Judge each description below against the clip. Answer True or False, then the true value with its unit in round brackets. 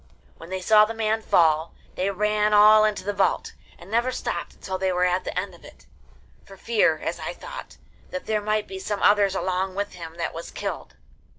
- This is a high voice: True (195 Hz)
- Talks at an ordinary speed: False (210 wpm)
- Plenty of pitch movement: False (2.7 semitones)